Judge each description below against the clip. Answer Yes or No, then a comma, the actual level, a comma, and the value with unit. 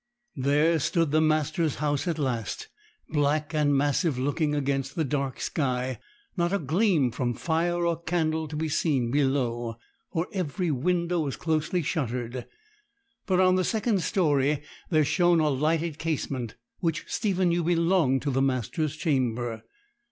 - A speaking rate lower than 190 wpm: Yes, average, 150 wpm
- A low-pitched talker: No, medium, 155 Hz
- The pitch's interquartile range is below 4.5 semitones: Yes, average, 3.7 semitones